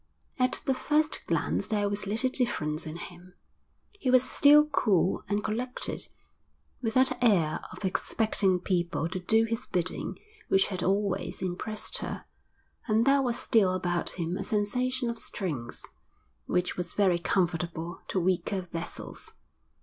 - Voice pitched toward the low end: No, high, 200 Hz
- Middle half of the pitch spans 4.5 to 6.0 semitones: Yes, average, 4.8 semitones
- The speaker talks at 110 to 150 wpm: Yes, average, 145 wpm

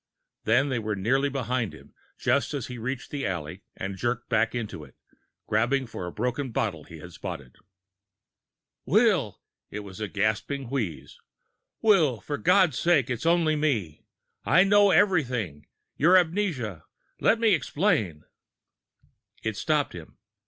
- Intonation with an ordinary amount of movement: No, wide, 7.2 semitones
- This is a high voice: No, low, 125 Hz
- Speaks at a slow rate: No, average, 145 wpm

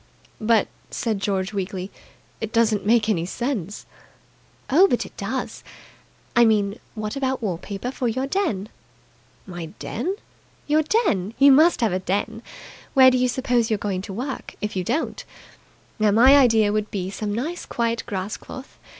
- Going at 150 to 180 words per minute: Yes, average, 165 wpm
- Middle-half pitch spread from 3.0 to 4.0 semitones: No, average, 4.4 semitones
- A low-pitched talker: No, high, 220 Hz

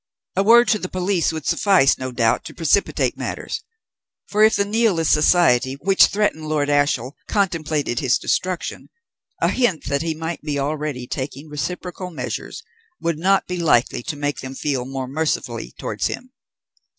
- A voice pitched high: No, medium, 155 Hz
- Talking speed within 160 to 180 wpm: Yes, average, 165 wpm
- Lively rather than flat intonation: No, average, 4.8 semitones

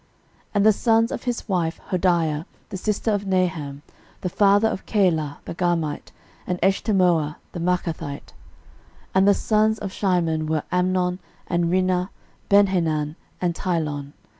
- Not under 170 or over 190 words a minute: No, average, 145 wpm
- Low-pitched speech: No, medium, 180 Hz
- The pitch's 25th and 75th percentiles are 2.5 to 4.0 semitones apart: Yes, average, 3.3 semitones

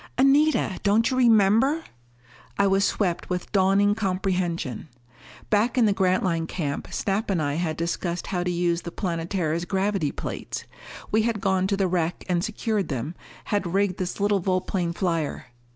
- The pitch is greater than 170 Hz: Yes, high, 190 Hz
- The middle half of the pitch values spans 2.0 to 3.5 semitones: Yes, average, 3.0 semitones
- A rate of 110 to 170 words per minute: Yes, average, 160 wpm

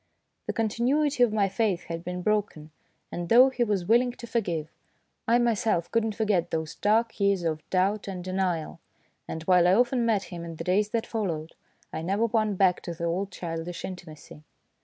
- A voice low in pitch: No, high, 195 Hz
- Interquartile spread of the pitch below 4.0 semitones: No, average, 4.6 semitones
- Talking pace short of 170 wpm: No, average, 190 wpm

